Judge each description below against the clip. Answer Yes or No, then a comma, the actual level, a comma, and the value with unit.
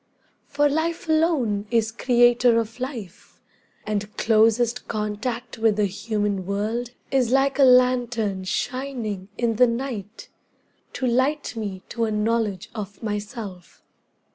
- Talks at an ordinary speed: No, slow, 125 wpm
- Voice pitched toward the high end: Yes, high, 230 Hz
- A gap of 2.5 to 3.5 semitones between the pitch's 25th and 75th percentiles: Yes, average, 3.2 semitones